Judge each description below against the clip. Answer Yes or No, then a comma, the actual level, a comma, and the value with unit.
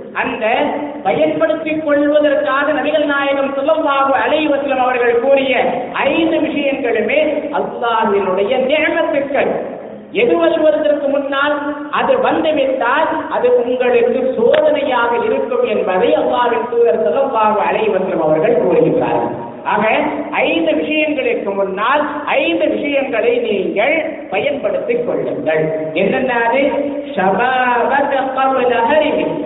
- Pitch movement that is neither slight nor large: Yes, average, 4.2 semitones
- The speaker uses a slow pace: Yes, slow, 80 wpm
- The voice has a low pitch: No, very high, 275 Hz